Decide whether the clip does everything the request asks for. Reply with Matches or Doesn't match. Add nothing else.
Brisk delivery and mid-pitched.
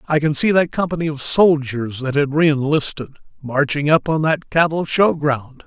Doesn't match